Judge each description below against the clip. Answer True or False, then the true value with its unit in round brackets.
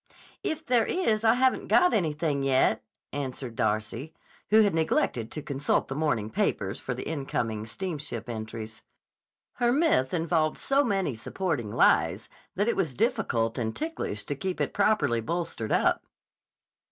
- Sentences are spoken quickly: False (150 wpm)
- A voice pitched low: False (150 Hz)